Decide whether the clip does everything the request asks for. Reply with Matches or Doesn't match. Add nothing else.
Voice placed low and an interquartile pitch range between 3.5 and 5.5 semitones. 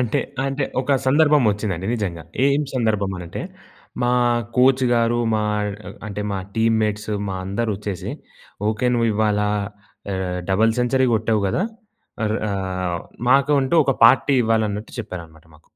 Matches